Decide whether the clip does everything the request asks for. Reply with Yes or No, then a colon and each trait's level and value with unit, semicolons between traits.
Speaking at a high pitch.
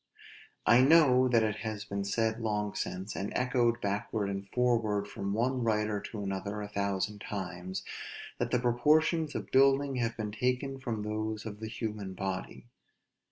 No: low, 110 Hz